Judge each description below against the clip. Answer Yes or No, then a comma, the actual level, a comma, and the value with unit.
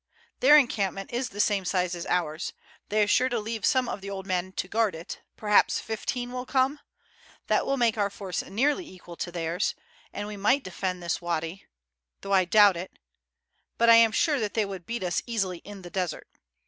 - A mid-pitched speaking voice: No, high, 200 Hz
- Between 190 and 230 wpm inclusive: Yes, fast, 205 wpm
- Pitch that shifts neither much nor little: Yes, average, 4.2 semitones